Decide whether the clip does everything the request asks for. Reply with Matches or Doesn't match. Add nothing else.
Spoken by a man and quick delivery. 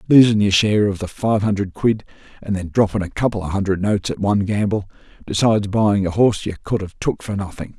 Matches